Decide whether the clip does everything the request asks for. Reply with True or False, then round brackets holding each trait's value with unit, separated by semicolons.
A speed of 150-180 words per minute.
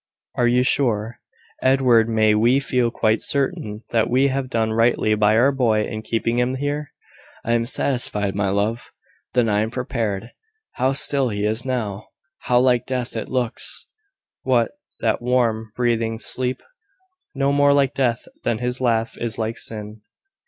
True (160 wpm)